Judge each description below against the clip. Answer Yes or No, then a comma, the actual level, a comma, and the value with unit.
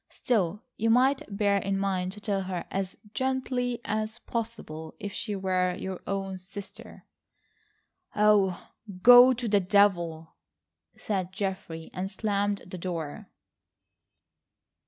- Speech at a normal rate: No, slow, 120 wpm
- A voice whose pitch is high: Yes, high, 200 Hz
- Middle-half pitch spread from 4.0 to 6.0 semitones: No, average, 2.8 semitones